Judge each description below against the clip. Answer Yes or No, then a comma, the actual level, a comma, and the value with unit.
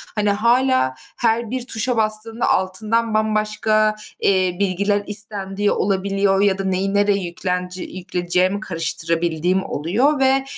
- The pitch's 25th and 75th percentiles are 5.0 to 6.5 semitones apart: No, average, 2.7 semitones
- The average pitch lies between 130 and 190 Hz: No, high, 200 Hz